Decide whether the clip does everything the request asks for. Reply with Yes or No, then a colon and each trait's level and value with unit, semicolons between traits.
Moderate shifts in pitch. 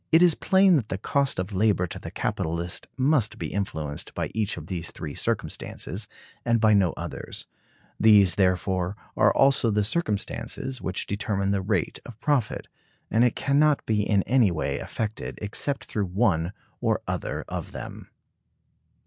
Yes: average, 4.8 semitones